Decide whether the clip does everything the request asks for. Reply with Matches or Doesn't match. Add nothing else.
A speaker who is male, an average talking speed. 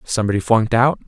Matches